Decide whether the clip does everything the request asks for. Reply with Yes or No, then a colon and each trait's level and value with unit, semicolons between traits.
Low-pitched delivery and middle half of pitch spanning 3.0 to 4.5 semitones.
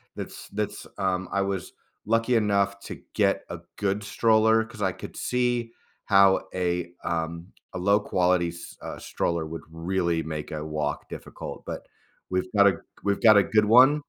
Yes: low, 100 Hz; average, 3.8 semitones